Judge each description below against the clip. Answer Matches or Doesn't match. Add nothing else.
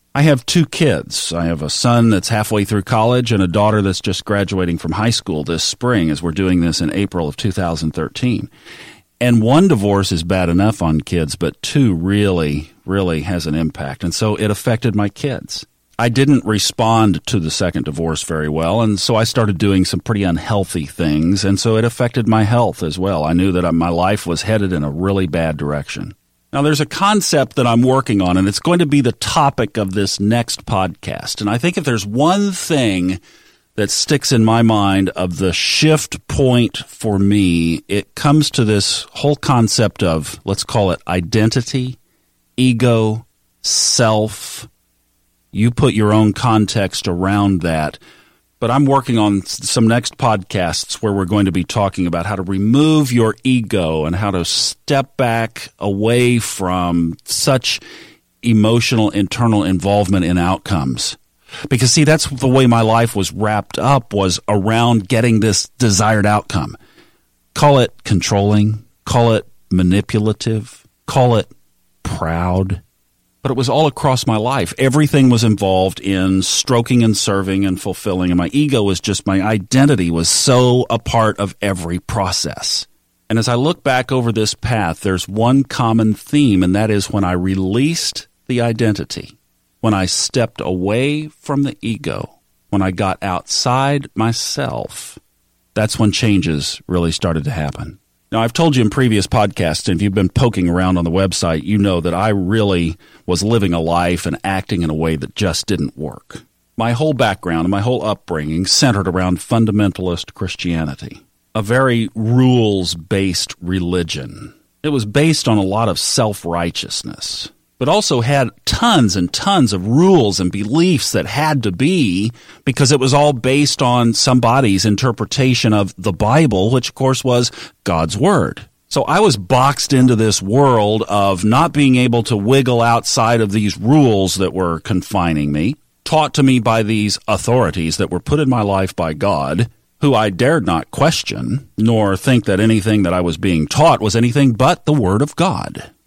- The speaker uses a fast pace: Doesn't match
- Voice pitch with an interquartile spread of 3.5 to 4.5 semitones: Doesn't match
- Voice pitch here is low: Matches